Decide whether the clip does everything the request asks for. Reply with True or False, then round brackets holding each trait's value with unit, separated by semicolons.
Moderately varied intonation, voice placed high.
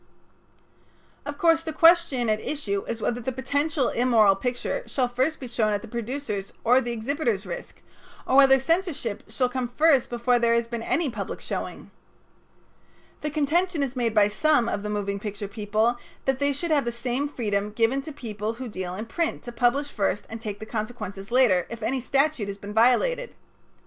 True (4.7 semitones; 240 Hz)